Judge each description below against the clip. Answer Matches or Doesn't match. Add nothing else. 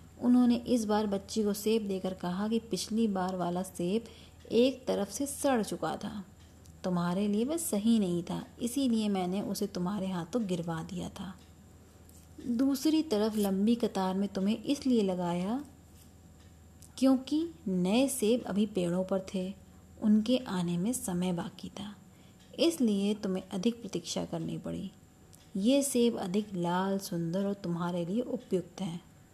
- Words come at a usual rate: Matches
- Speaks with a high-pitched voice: Matches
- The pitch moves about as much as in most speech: Matches